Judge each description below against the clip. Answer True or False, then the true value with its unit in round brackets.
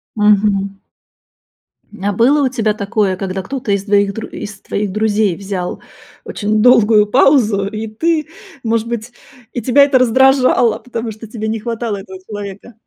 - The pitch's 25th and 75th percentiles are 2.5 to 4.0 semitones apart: True (2.9 semitones)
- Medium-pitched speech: False (215 Hz)